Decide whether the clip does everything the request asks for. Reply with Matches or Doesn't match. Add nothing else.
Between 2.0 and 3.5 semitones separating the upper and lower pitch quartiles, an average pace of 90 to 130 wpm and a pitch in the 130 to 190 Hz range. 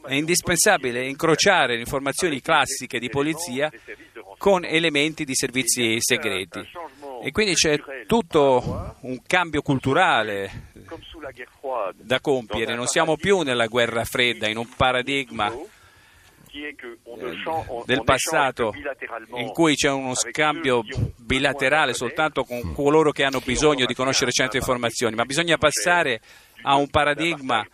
Doesn't match